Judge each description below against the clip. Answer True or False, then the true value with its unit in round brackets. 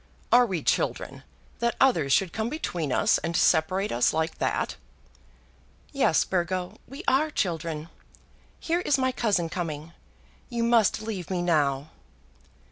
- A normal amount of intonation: False (6.6 semitones)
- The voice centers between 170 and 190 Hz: True (185 Hz)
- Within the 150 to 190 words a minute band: False (135 wpm)